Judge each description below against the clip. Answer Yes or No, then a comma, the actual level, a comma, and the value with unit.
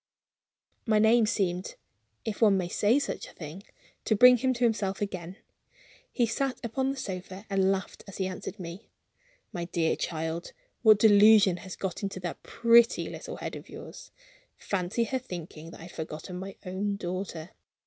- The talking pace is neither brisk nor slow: Yes, average, 170 wpm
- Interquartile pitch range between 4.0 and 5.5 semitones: No, average, 3.6 semitones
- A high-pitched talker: Yes, high, 195 Hz